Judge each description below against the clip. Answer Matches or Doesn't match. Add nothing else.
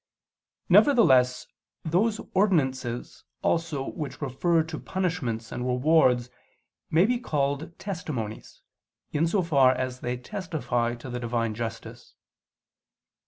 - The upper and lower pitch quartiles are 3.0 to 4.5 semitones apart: Doesn't match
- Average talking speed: Doesn't match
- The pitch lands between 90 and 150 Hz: Matches